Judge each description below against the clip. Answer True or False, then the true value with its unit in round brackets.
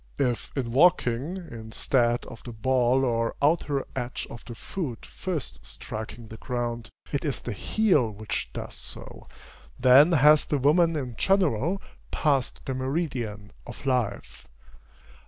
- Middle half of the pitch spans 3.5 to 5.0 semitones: True (4.1 semitones)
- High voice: False (130 Hz)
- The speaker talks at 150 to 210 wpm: False (135 wpm)